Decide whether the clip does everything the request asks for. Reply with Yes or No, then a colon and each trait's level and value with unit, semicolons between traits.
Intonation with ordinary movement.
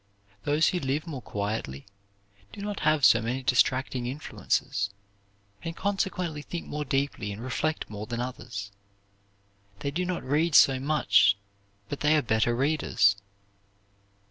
Yes: average, 4.9 semitones